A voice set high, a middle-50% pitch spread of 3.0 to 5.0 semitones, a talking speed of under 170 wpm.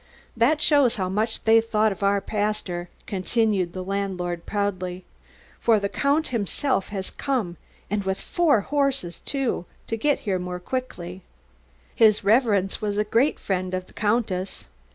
Yes: high, 205 Hz; average, 3.8 semitones; average, 155 wpm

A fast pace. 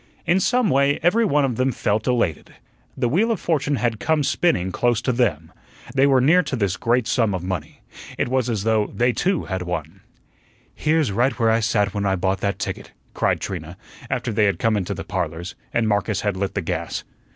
Yes: fast, 210 wpm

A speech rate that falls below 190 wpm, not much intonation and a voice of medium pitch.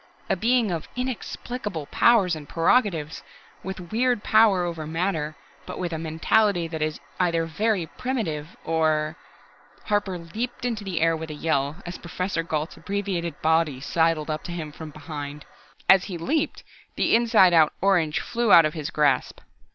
No: average, 165 wpm; average, 4.6 semitones; medium, 170 Hz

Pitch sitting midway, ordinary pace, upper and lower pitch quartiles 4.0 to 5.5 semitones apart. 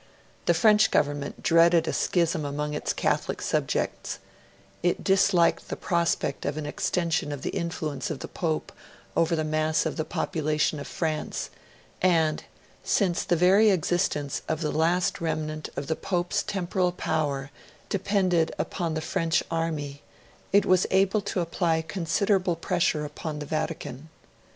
No: medium, 165 Hz; average, 145 wpm; narrow, 2.6 semitones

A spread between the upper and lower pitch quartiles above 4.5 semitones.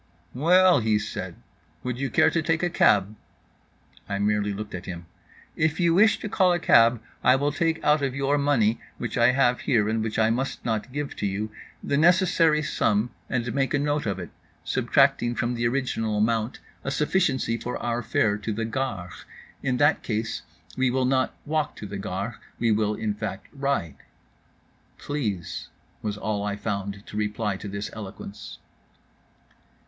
Yes: average, 5.2 semitones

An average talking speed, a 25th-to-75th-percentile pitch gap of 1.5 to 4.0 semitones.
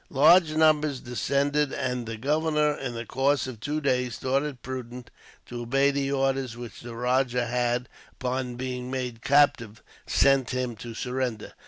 Yes: average, 165 wpm; narrow, 2.5 semitones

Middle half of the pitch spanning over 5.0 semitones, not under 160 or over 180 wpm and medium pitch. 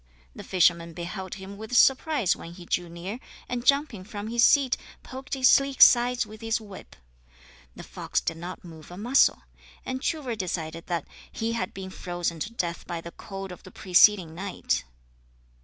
No: wide, 5.4 semitones; average, 175 wpm; high, 195 Hz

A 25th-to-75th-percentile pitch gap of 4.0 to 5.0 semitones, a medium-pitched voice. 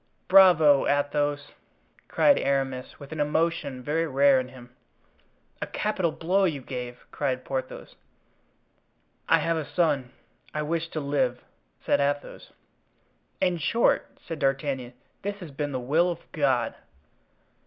No: average, 3.6 semitones; medium, 145 Hz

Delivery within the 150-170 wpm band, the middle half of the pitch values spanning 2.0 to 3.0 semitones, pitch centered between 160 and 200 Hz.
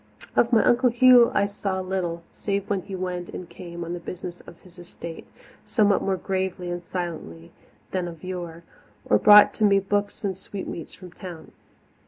No: average, 180 wpm; narrow, 2.5 semitones; medium, 185 Hz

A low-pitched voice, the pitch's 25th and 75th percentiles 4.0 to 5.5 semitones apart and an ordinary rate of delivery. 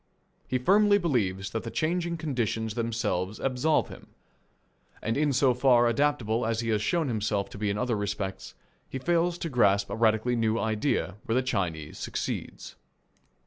Yes: low, 115 Hz; average, 4.7 semitones; average, 165 wpm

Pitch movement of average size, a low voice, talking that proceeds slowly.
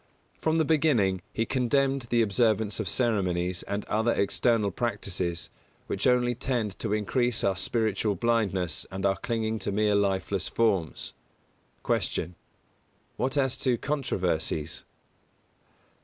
Yes: average, 4.1 semitones; low, 110 Hz; slow, 125 wpm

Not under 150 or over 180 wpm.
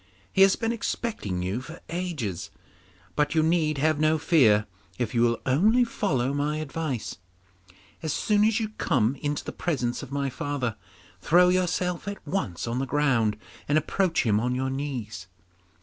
Yes: average, 165 wpm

